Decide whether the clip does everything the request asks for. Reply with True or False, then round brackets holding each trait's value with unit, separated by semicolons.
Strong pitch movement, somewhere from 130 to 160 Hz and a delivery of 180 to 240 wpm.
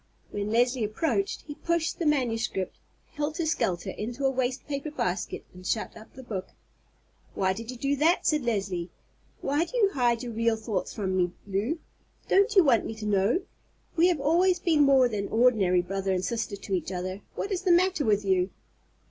False (7.3 semitones; 235 Hz; 190 wpm)